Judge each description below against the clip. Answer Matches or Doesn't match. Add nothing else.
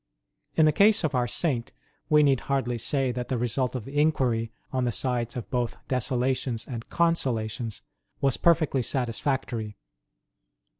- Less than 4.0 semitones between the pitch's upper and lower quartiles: Matches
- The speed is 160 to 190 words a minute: Doesn't match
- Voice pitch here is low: Matches